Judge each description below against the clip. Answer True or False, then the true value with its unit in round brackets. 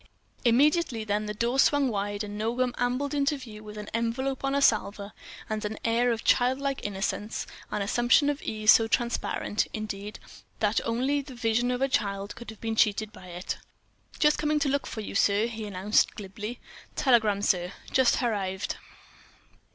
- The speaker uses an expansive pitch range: False (3.5 semitones)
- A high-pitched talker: True (225 Hz)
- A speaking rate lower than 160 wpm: False (170 wpm)